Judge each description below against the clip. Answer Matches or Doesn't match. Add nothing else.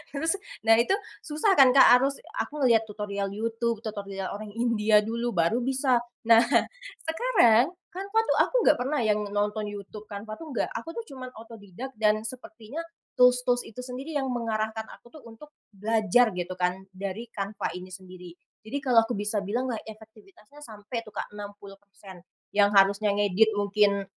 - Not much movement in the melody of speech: Doesn't match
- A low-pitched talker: Doesn't match